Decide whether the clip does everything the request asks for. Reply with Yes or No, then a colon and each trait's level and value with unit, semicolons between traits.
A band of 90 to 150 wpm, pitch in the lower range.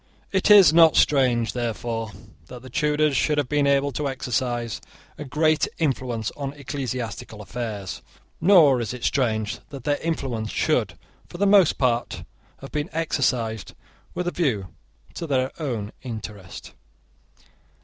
Yes: average, 140 wpm; low, 130 Hz